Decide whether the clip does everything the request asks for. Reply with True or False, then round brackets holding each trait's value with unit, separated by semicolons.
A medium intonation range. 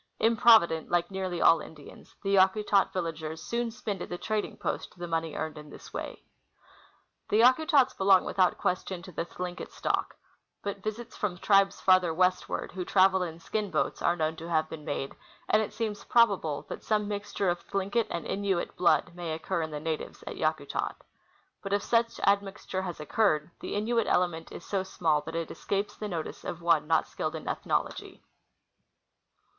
True (3.8 semitones)